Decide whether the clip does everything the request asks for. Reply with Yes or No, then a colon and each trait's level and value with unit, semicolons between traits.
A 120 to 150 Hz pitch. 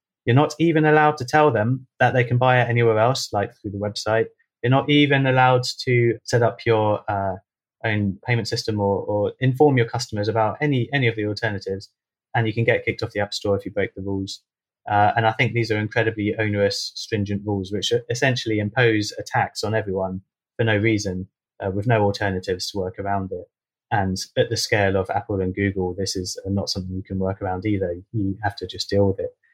No: low, 110 Hz